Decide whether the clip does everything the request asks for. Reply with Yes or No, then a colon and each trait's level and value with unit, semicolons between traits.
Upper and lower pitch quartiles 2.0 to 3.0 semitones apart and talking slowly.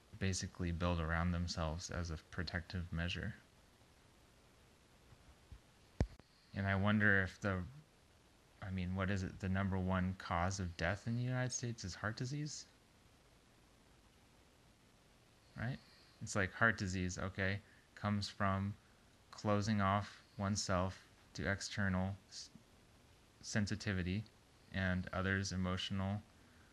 Yes: narrow, 2.6 semitones; slow, 110 wpm